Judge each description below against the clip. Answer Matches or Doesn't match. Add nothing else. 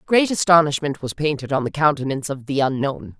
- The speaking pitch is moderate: Matches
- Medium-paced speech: Matches